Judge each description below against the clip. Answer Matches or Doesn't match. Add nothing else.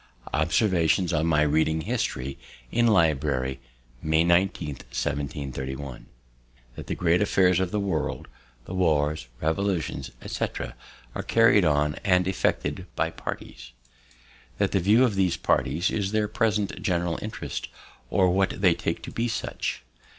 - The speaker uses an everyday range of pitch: Matches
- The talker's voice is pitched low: Matches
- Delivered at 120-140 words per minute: Matches